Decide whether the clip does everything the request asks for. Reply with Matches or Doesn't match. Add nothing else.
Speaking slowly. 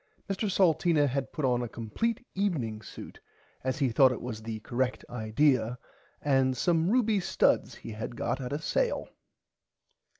Doesn't match